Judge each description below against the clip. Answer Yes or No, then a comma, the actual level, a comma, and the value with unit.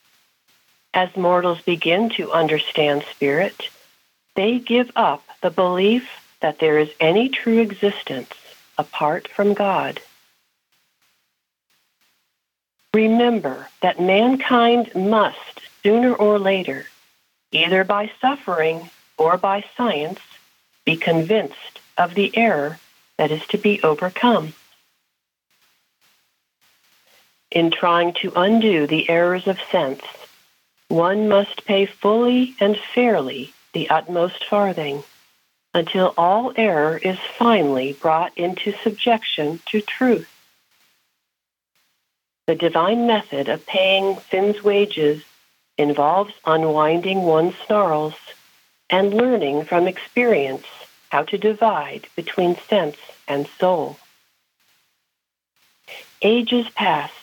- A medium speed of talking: No, slow, 100 wpm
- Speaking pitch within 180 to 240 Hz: Yes, high, 190 Hz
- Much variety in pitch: No, average, 5.0 semitones